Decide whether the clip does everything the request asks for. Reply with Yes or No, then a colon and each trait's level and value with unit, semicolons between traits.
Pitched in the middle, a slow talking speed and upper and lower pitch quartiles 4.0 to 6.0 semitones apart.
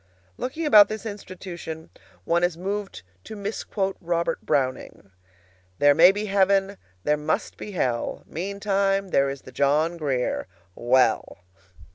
Yes: medium, 175 Hz; slow, 130 wpm; wide, 5.6 semitones